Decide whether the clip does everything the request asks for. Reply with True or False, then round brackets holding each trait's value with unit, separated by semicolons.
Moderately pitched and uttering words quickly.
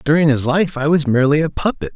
True (150 Hz; 245 wpm)